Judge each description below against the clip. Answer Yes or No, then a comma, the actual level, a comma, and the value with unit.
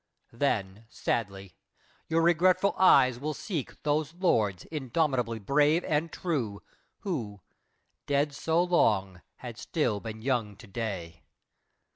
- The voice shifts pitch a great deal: Yes, wide, 7.2 semitones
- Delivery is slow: Yes, slow, 115 wpm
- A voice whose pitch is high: No, low, 130 Hz